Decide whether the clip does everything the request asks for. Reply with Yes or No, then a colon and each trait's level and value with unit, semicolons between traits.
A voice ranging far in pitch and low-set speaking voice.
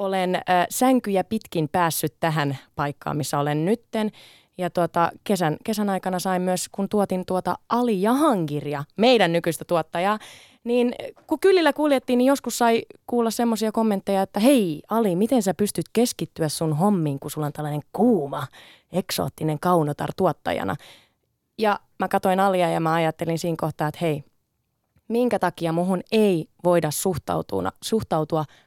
No: wide, 5.7 semitones; medium, 180 Hz